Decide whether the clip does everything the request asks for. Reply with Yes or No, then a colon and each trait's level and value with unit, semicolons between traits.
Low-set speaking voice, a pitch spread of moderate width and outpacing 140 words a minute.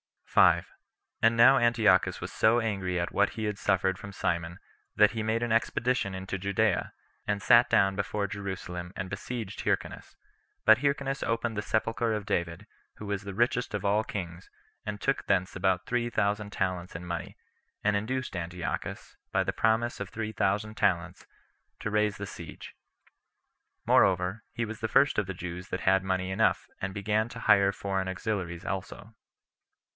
Yes: low, 100 Hz; average, 3.0 semitones; average, 170 wpm